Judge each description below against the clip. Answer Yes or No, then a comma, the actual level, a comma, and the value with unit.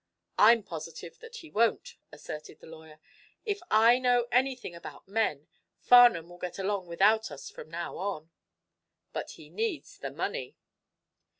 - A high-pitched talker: Yes, high, 200 Hz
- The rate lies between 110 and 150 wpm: Yes, average, 145 wpm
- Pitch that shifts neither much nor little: No, wide, 6.6 semitones